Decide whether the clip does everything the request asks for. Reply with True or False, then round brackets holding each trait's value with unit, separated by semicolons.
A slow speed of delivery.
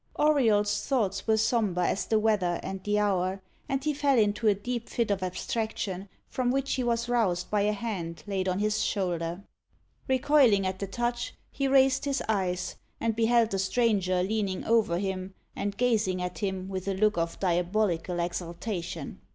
False (175 wpm)